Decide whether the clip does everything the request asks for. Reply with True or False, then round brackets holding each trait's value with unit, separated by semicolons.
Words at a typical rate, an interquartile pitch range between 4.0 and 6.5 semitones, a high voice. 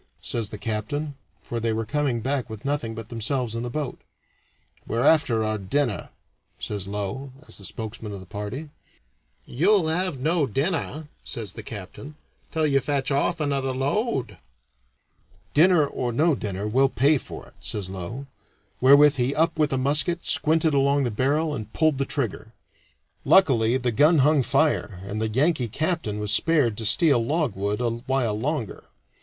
False (165 wpm; 5.2 semitones; 130 Hz)